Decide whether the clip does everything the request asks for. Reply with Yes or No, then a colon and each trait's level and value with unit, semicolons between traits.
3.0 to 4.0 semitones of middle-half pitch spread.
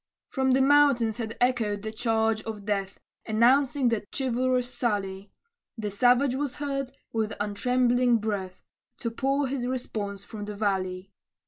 Yes: average, 3.7 semitones